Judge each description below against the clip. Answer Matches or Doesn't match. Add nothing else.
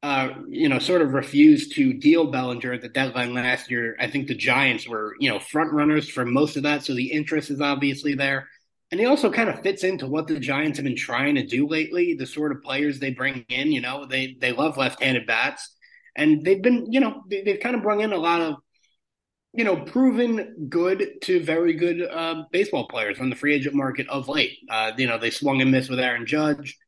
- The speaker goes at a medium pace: Doesn't match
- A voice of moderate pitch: Matches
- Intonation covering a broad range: Matches